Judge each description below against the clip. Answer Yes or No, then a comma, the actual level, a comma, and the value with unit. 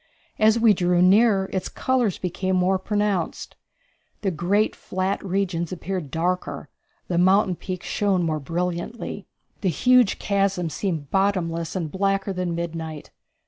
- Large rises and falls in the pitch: No, narrow, 2.5 semitones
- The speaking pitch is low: No, medium, 185 Hz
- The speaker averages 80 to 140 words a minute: Yes, slow, 135 wpm